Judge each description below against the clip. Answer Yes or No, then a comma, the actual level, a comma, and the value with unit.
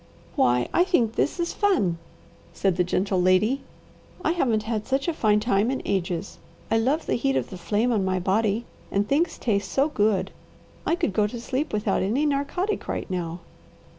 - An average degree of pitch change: No, wide, 6.2 semitones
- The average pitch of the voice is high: Yes, high, 215 Hz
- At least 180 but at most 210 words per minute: Yes, average, 190 wpm